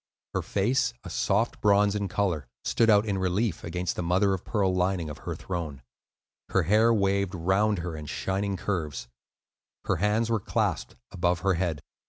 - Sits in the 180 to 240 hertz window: No, very low, 95 Hz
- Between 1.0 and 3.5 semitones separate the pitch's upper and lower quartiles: Yes, average, 2.8 semitones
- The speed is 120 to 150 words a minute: No, average, 175 wpm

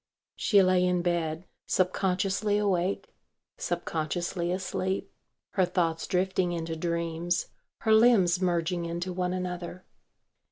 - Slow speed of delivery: Yes, slow, 110 wpm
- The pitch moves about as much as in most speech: No, narrow, 1.6 semitones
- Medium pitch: Yes, medium, 180 Hz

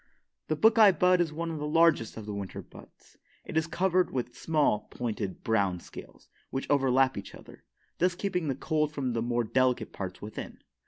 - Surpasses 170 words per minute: Yes, average, 190 wpm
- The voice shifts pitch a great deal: Yes, wide, 6.6 semitones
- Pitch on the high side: No, low, 135 Hz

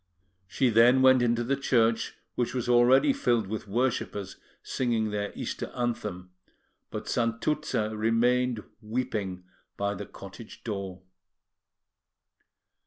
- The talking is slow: Yes, slow, 110 wpm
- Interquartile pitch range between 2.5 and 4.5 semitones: Yes, average, 3.0 semitones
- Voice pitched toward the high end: No, low, 115 Hz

